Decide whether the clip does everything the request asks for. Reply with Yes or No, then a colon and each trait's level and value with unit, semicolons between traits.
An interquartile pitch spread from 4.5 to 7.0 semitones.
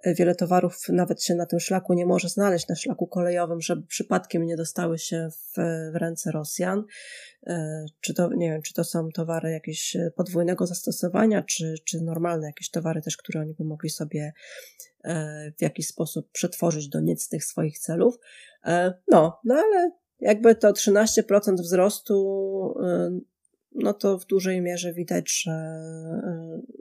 No: narrow, 2.6 semitones